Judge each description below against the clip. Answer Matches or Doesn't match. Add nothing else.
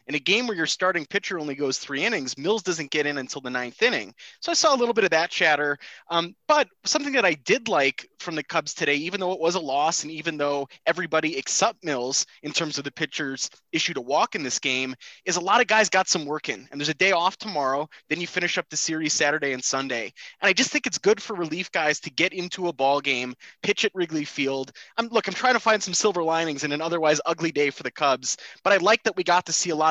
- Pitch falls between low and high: Matches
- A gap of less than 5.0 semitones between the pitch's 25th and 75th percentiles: Matches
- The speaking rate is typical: Doesn't match